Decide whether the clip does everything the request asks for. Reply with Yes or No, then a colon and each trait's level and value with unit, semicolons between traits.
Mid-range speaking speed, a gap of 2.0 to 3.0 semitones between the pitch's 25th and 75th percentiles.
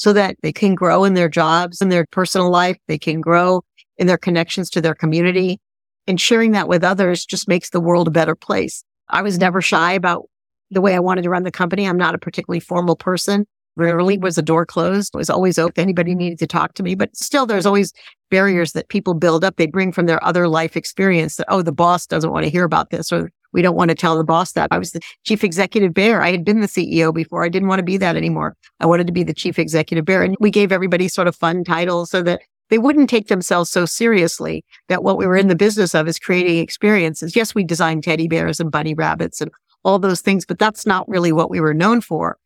No: fast, 250 wpm; narrow, 2.5 semitones